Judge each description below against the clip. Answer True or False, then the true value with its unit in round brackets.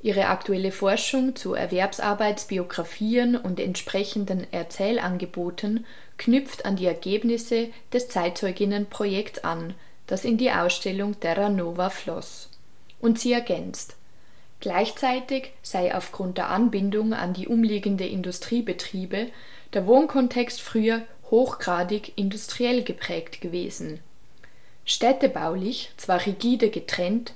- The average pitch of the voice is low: False (205 Hz)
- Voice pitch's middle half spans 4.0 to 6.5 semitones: True (4.3 semitones)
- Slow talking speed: True (100 wpm)